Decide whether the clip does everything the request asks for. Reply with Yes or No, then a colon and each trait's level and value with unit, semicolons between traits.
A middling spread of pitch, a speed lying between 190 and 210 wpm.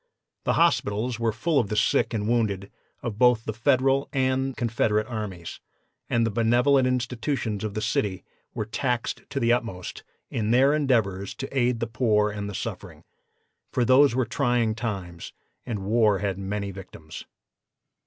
No: average, 3.4 semitones; average, 160 wpm